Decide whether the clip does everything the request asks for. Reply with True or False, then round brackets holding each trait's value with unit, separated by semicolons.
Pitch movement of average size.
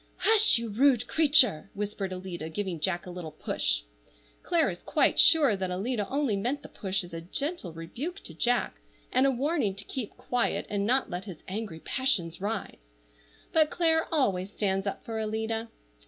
False (6.4 semitones)